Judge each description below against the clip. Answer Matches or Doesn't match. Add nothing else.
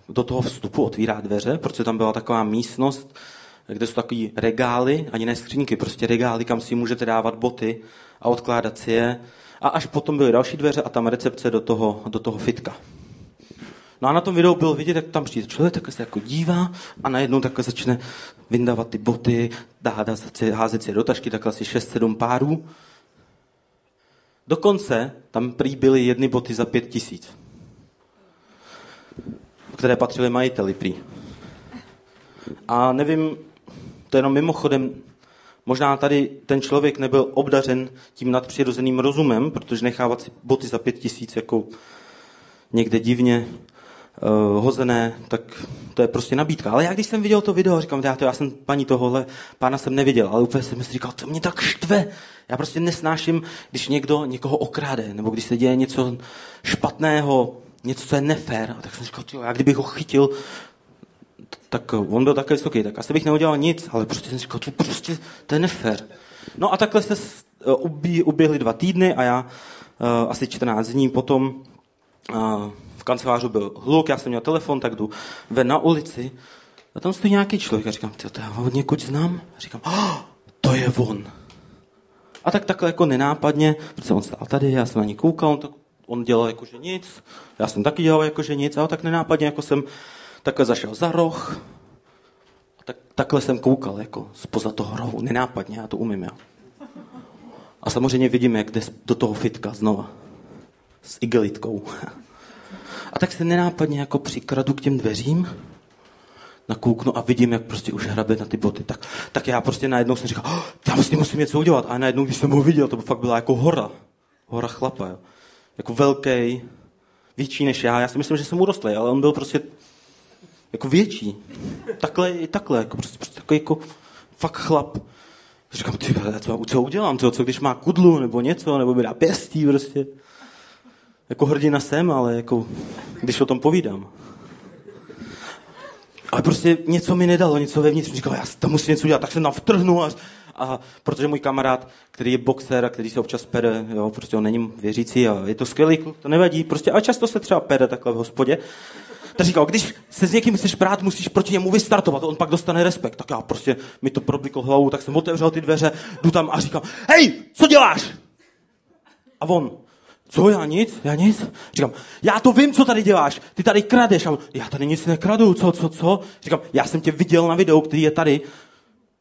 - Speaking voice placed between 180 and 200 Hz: Doesn't match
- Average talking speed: Doesn't match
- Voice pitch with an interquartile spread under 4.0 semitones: Doesn't match